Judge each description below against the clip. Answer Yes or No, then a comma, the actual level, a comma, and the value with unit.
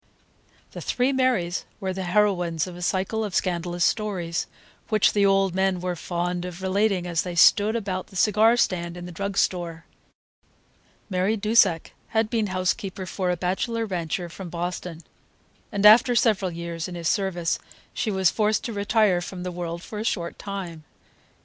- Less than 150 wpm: No, average, 170 wpm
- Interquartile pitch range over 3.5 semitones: No, average, 3.1 semitones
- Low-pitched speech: No, medium, 185 Hz